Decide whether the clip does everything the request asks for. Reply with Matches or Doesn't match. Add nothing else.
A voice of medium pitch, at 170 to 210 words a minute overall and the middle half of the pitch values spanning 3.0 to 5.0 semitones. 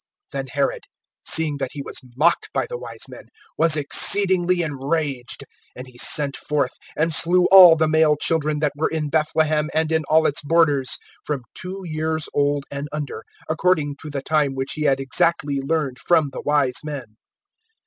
Doesn't match